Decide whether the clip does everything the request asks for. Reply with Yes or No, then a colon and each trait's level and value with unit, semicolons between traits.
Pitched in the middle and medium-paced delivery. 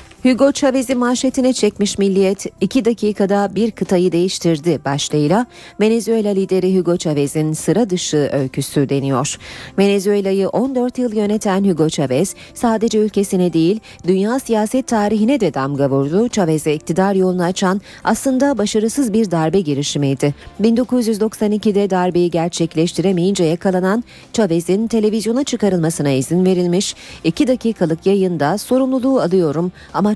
No: high, 195 Hz; average, 115 wpm